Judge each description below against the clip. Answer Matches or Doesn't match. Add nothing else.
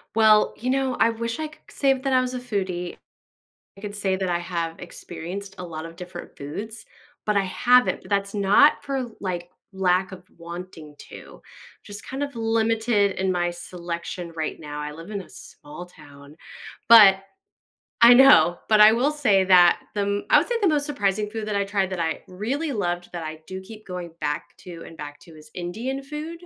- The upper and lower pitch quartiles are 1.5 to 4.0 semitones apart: Doesn't match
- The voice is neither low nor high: Doesn't match